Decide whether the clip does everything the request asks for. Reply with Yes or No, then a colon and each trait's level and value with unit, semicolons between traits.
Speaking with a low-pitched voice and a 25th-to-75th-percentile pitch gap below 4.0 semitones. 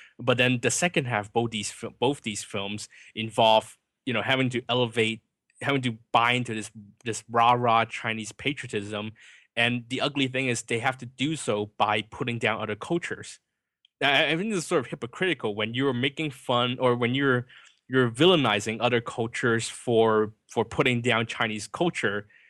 Yes: low, 120 Hz; average, 2.8 semitones